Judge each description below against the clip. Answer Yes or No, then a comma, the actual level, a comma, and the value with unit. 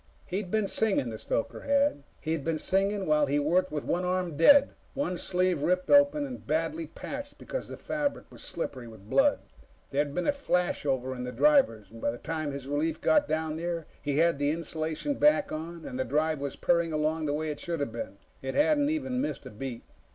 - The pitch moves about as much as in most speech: No, wide, 6.5 semitones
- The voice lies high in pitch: No, medium, 165 Hz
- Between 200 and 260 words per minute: Yes, fast, 205 wpm